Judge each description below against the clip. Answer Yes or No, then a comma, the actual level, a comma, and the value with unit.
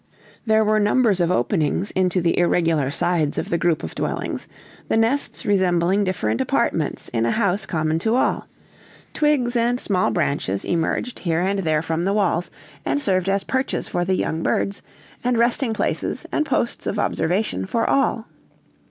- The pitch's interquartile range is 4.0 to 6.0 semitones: Yes, average, 5.0 semitones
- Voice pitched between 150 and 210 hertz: Yes, medium, 185 Hz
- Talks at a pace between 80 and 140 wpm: No, average, 170 wpm